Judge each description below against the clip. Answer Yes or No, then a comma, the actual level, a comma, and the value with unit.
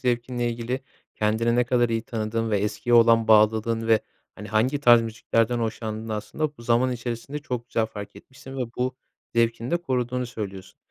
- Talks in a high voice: No, low, 115 Hz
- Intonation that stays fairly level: Yes, narrow, 1.9 semitones